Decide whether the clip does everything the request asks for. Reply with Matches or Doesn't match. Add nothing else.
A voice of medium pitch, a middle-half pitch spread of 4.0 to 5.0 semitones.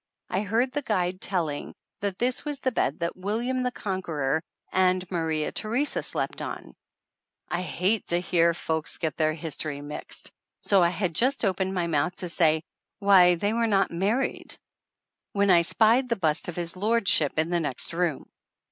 Matches